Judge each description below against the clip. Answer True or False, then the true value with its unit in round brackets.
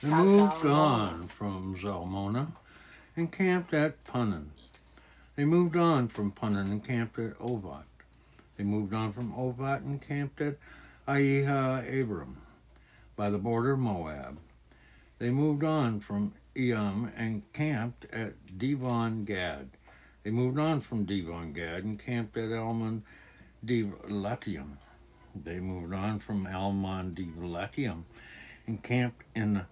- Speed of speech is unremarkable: False (125 wpm)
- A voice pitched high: False (110 Hz)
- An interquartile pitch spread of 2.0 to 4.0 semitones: False (5.5 semitones)